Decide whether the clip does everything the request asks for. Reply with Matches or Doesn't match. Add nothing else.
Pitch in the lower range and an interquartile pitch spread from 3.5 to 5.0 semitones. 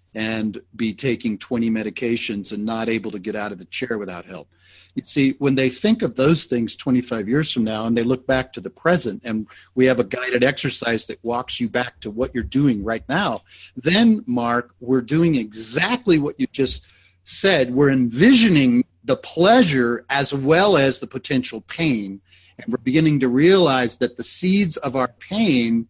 Matches